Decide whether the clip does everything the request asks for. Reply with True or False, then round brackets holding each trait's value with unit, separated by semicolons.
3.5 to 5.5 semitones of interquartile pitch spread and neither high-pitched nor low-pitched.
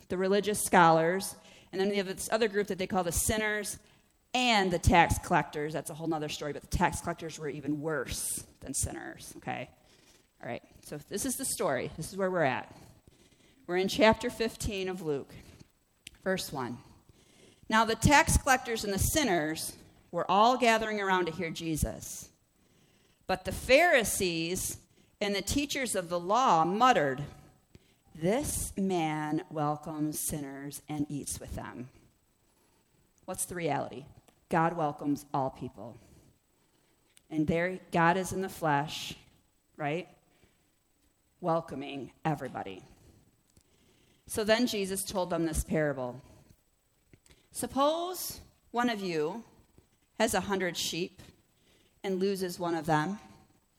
True (4.8 semitones; 175 Hz)